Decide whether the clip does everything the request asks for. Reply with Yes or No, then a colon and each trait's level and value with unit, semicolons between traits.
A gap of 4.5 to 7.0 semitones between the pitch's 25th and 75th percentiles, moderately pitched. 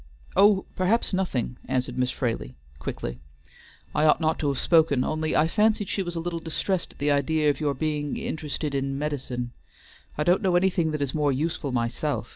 No: average, 4.0 semitones; medium, 150 Hz